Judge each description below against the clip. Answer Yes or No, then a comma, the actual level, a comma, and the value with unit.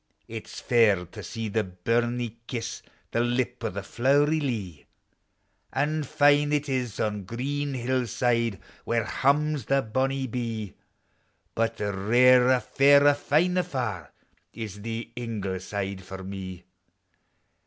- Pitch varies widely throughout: No, average, 4.4 semitones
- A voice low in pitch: Yes, low, 120 Hz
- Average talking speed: No, slow, 125 wpm